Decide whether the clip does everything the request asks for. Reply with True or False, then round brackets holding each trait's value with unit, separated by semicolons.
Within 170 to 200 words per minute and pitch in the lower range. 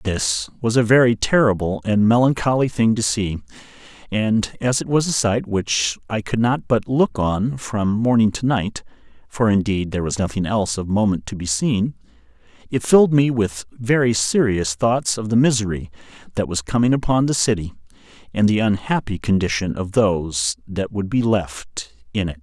True (175 wpm; 110 Hz)